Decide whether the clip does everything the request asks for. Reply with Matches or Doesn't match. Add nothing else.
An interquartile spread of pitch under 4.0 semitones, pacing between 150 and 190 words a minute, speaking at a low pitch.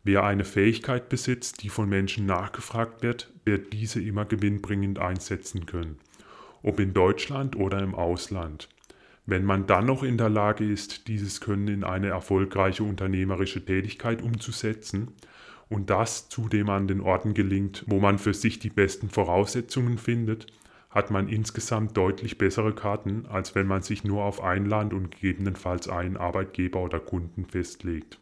Matches